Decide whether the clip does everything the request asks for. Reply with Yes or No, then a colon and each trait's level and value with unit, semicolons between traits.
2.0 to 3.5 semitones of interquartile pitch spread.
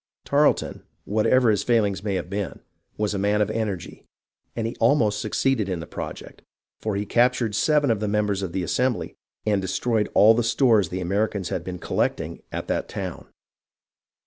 Yes: average, 2.8 semitones